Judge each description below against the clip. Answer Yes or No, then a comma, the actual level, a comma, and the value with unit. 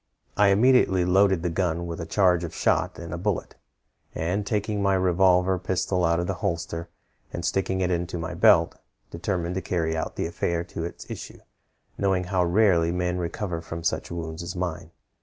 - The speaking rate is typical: Yes, average, 185 wpm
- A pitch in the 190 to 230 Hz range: No, very low, 90 Hz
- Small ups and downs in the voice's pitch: Yes, narrow, 2.0 semitones